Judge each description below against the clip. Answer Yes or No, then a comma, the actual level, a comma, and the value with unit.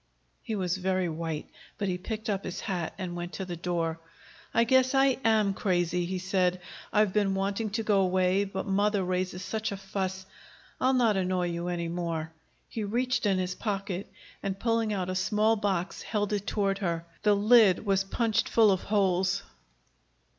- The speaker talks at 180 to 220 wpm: Yes, average, 185 wpm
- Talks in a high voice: Yes, high, 195 Hz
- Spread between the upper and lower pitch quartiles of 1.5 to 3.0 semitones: Yes, average, 2.7 semitones